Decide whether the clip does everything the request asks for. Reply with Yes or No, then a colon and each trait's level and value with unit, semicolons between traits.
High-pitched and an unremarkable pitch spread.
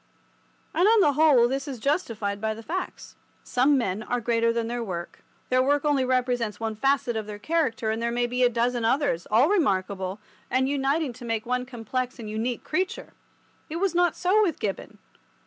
Yes: high, 245 Hz; average, 4.1 semitones